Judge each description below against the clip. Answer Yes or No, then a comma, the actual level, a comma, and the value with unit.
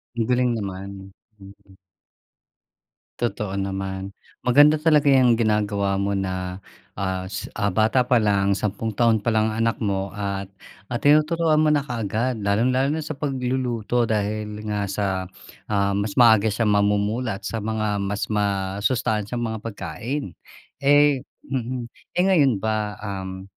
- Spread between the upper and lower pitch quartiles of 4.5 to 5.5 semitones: No, average, 3.8 semitones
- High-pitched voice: No, low, 110 Hz